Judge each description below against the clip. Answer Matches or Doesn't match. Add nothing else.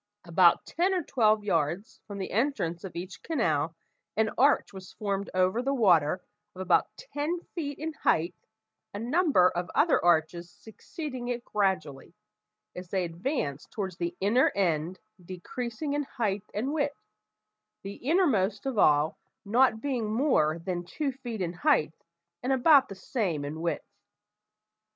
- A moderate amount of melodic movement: Doesn't match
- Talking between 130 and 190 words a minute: Matches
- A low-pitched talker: Doesn't match